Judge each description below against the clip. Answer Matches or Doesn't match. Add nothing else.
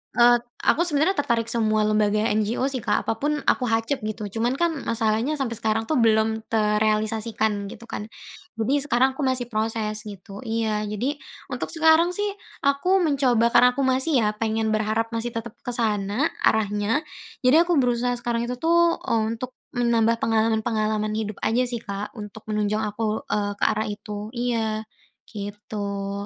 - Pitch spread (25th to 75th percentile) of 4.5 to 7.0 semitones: Doesn't match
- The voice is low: Doesn't match